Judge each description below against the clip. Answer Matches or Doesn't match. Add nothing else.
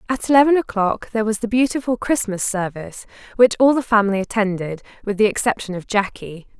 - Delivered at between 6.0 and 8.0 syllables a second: Matches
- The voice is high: Matches